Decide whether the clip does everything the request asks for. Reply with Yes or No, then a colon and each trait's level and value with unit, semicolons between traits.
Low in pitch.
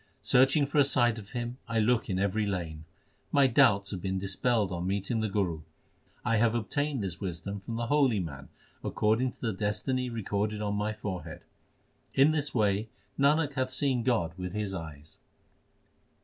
Yes: low, 110 Hz